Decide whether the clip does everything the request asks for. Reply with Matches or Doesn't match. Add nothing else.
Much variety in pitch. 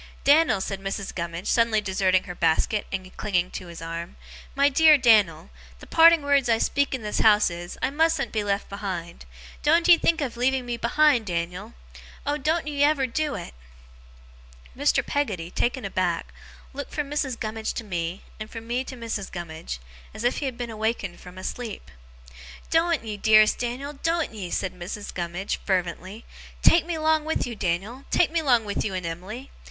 Matches